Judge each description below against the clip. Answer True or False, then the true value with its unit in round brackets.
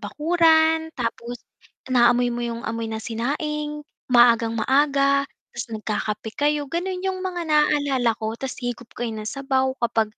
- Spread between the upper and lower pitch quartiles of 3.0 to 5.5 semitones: True (4.4 semitones)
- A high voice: True (260 Hz)